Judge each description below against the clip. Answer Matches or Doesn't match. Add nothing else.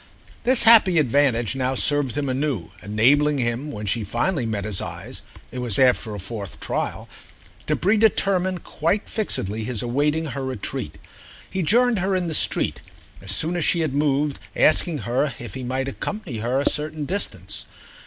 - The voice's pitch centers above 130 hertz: Matches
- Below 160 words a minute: Doesn't match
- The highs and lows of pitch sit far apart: Matches